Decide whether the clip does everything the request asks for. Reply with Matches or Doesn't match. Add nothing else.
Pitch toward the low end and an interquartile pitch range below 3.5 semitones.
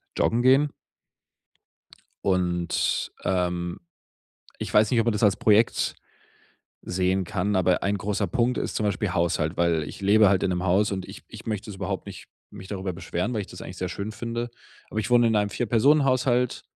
Doesn't match